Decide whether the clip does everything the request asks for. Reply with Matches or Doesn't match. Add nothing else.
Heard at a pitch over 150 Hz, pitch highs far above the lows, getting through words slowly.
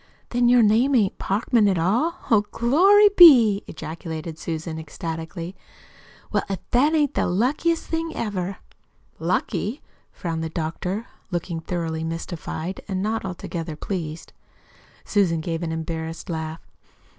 Matches